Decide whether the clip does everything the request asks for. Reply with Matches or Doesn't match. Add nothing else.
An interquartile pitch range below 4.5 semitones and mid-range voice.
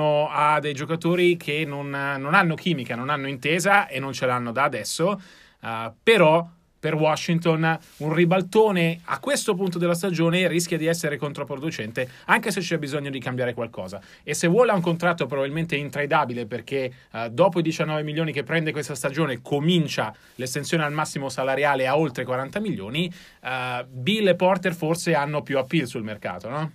Matches